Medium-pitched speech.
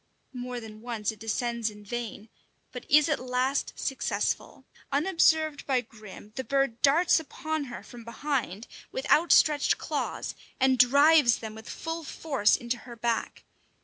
No: very high, 250 Hz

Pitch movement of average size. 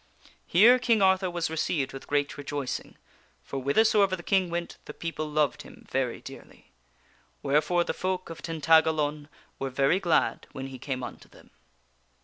Yes: average, 4.4 semitones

